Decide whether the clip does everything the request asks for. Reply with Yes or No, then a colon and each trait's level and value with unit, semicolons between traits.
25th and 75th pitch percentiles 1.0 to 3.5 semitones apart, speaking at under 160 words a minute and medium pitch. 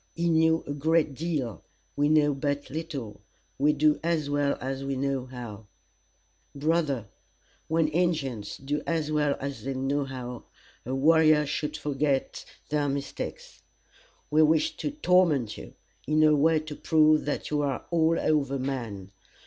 Yes: narrow, 2.5 semitones; average, 150 wpm; medium, 145 Hz